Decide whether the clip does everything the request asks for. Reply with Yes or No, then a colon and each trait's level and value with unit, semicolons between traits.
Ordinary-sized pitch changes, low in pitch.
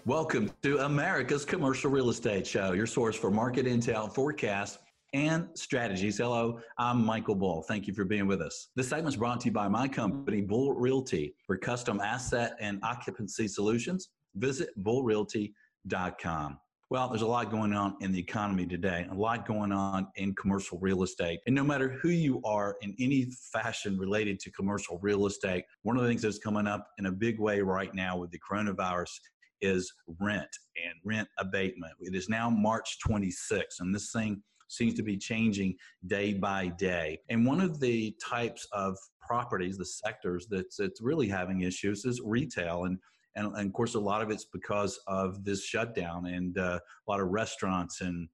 Yes: average, 3.6 semitones; low, 105 Hz